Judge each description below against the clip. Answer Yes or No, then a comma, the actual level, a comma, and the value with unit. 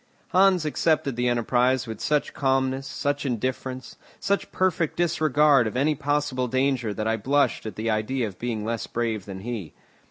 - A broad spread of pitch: No, average, 4.0 semitones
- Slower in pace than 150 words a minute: No, average, 165 wpm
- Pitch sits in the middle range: No, low, 130 Hz